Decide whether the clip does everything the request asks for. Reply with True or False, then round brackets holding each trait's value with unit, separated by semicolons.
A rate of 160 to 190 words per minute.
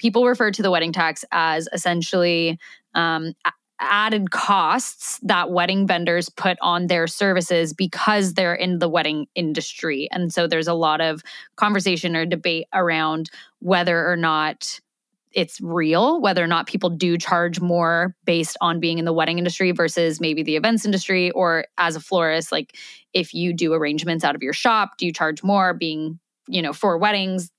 True (175 wpm)